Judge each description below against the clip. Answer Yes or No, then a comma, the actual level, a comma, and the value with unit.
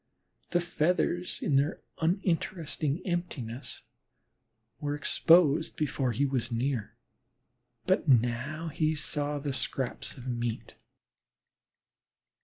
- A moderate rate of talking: No, slow, 95 wpm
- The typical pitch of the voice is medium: Yes, medium, 145 Hz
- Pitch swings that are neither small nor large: Yes, average, 4.4 semitones